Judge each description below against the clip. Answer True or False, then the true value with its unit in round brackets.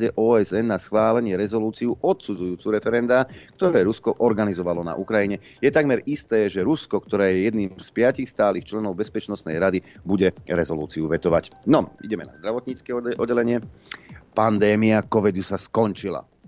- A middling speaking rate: True (135 wpm)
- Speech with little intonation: False (3.4 semitones)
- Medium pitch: False (105 Hz)